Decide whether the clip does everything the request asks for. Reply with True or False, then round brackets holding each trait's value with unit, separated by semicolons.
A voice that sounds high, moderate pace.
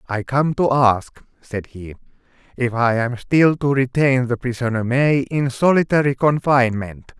False (130 Hz; 150 wpm)